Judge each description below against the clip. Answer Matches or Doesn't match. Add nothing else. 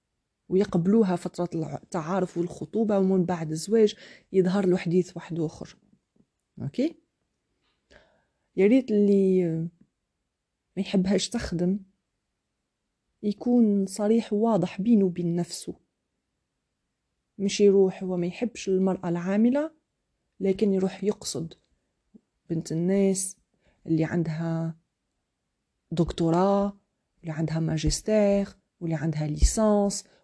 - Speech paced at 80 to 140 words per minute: Matches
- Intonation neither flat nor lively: Matches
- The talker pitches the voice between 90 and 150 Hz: Doesn't match